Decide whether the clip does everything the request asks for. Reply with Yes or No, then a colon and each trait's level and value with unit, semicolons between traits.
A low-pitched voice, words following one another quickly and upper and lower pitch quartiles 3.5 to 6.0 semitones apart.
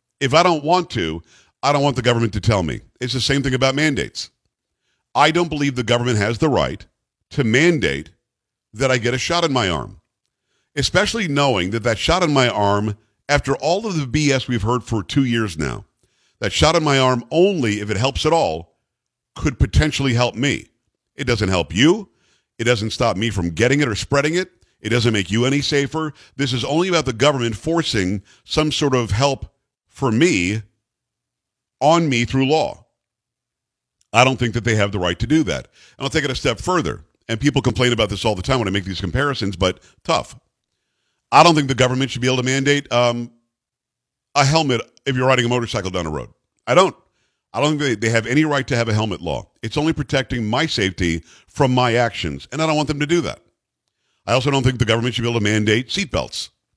Yes: low, 125 Hz; fast, 215 wpm; average, 4.2 semitones